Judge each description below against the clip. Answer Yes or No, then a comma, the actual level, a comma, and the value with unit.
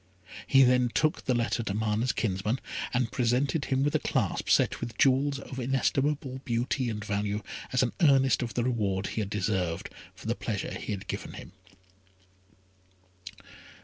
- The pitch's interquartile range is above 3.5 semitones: Yes, average, 3.9 semitones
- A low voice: Yes, low, 125 Hz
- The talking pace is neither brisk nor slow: Yes, average, 165 wpm